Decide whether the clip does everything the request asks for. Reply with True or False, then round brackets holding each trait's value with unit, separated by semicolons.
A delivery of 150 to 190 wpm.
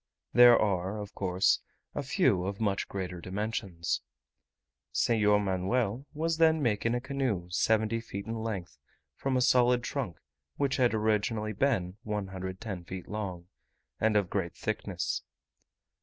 False (135 wpm)